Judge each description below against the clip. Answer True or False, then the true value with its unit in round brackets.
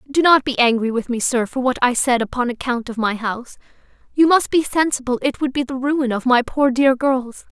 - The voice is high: True (255 Hz)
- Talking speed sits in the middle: False (235 wpm)